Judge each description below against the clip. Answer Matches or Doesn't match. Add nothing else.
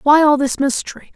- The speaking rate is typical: Doesn't match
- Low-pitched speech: Doesn't match